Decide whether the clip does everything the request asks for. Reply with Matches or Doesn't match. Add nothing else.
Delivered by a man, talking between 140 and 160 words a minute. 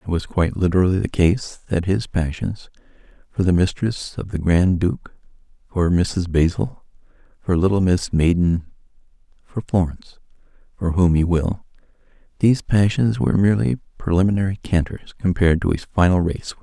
Matches